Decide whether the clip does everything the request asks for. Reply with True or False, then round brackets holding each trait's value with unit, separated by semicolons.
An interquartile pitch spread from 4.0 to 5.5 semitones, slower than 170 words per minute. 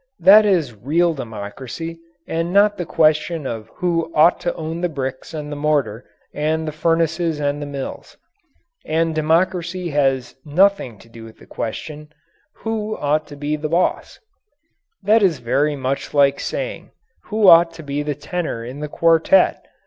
False (3.3 semitones; 160 wpm)